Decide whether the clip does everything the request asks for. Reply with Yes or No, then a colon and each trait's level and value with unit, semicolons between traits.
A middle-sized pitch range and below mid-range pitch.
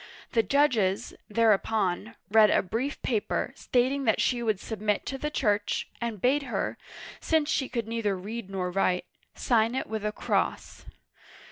No: average, 3.5 semitones; high, 225 Hz